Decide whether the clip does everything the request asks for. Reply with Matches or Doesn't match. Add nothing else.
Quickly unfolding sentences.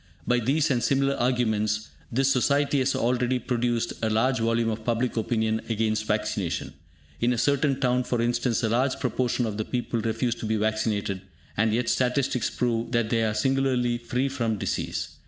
Doesn't match